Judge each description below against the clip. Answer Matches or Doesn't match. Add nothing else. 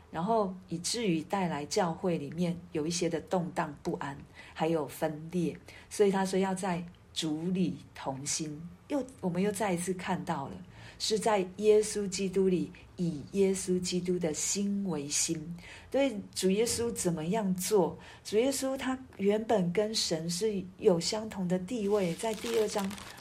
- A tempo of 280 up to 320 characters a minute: Doesn't match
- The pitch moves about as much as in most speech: Matches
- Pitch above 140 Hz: Matches